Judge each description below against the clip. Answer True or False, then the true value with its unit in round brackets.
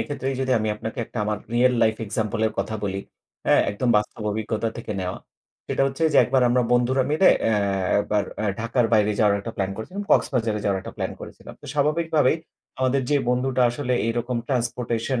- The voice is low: True (120 Hz)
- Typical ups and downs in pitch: True (3.3 semitones)